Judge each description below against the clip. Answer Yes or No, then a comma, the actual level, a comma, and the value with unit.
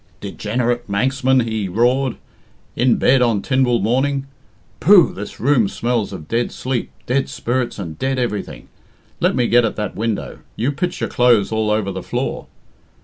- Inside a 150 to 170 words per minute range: Yes, average, 160 wpm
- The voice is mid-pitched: No, low, 120 Hz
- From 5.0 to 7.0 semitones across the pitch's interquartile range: No, average, 3.3 semitones